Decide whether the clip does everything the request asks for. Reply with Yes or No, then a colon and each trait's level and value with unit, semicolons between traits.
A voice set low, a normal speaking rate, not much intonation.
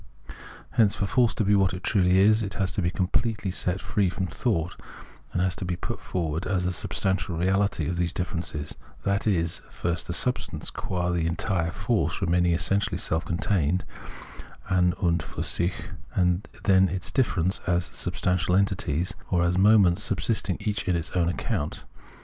Yes: very low, 90 Hz; average, 165 wpm; narrow, 2.2 semitones